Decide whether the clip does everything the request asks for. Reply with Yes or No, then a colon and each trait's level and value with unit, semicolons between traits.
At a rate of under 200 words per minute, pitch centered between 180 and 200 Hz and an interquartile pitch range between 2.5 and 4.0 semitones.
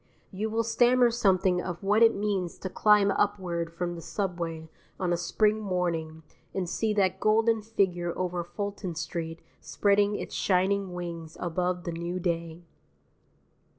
Yes: average, 150 wpm; medium, 185 Hz; average, 3.1 semitones